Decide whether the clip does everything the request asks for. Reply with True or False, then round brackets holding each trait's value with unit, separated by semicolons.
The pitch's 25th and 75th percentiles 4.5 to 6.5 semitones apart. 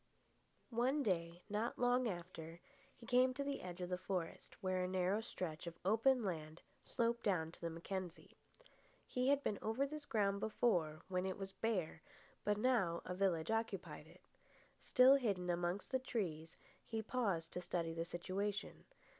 True (5.1 semitones)